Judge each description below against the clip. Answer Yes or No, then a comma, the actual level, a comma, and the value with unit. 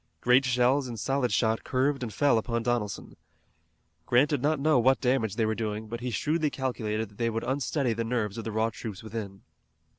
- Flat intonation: No, average, 3.1 semitones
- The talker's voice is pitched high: No, low, 120 Hz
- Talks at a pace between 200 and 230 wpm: Yes, fast, 205 wpm